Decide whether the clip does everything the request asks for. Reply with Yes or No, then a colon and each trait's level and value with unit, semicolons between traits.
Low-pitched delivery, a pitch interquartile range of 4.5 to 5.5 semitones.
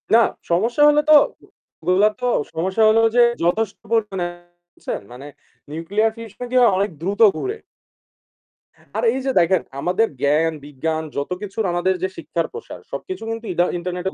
No: high, 190 Hz; average, 5.0 semitones